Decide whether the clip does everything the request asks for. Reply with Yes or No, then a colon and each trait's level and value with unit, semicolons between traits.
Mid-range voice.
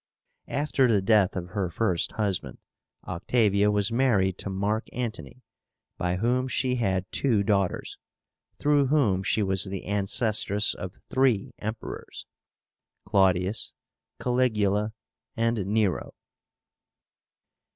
No: low, 105 Hz